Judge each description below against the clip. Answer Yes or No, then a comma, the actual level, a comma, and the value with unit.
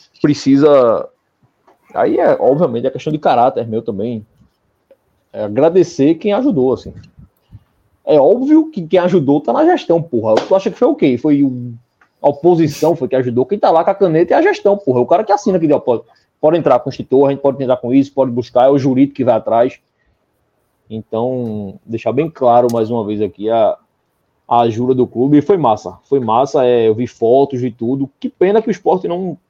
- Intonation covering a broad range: Yes, wide, 6.2 semitones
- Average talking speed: No, fast, 210 wpm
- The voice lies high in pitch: No, low, 135 Hz